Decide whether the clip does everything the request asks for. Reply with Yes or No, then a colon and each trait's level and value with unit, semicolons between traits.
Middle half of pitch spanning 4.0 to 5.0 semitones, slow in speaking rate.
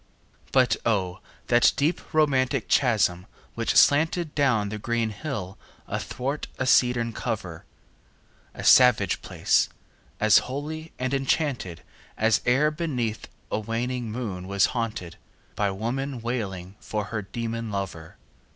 Yes: average, 4.5 semitones; slow, 125 wpm